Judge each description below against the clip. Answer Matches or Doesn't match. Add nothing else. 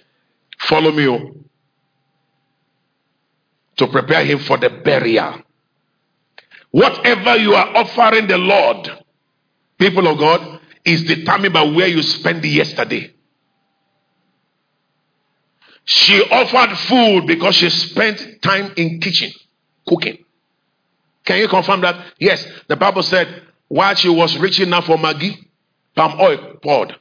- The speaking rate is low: Matches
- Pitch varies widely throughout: Doesn't match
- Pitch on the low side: Doesn't match